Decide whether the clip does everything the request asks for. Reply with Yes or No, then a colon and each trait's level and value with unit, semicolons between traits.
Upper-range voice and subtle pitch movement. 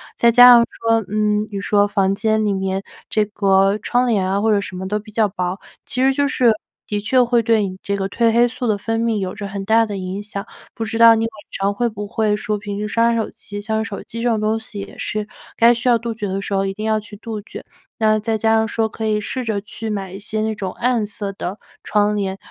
Yes: high, 215 Hz; narrow, 2.0 semitones